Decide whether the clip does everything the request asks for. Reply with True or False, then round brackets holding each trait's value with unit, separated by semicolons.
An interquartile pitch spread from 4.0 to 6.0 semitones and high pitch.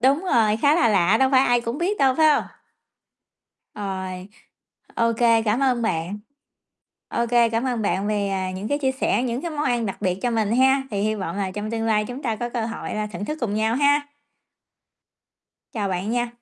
True (4.3 semitones; 230 Hz)